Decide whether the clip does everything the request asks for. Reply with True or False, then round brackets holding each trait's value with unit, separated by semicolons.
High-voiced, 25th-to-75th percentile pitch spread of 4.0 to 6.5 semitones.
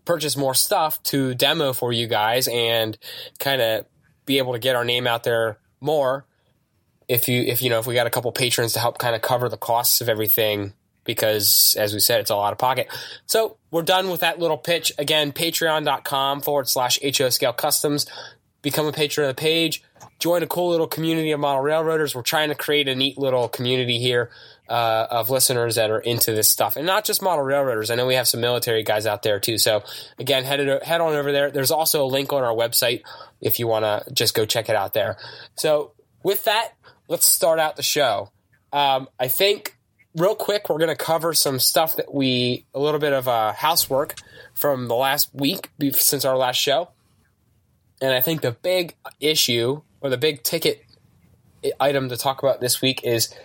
False (135 Hz; 4.5 semitones)